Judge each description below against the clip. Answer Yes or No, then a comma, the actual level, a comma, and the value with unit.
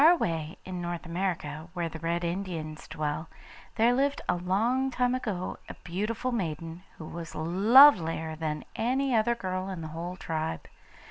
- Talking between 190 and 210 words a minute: No, average, 160 wpm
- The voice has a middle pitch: Yes, medium, 180 Hz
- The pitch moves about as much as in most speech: No, wide, 5.9 semitones